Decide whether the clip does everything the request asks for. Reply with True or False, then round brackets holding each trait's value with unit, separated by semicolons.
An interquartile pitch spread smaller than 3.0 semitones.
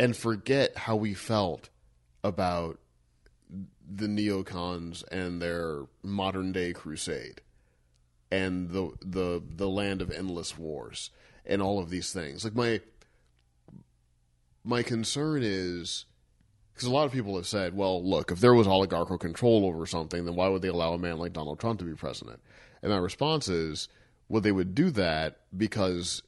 False (4.0 semitones)